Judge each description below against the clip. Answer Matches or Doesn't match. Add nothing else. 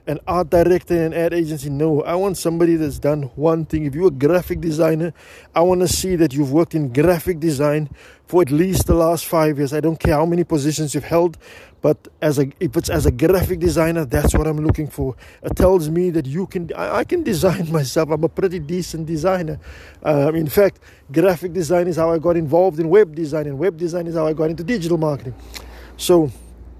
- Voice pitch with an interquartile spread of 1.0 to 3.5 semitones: Matches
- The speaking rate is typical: Doesn't match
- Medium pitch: Matches